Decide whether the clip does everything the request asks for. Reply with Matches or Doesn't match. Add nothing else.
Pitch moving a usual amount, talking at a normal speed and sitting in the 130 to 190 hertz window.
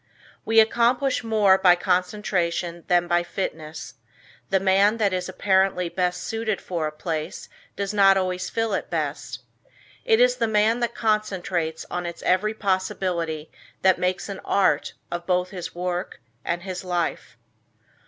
Matches